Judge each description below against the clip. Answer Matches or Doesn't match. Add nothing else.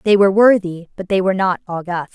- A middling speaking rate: Doesn't match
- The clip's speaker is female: Matches